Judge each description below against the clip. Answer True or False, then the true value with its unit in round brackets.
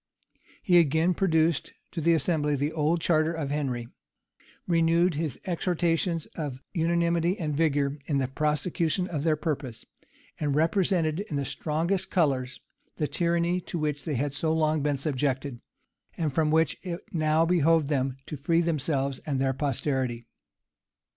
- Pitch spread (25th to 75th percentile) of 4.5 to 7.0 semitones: False (2.9 semitones)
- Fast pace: False (150 wpm)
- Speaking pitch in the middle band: True (155 Hz)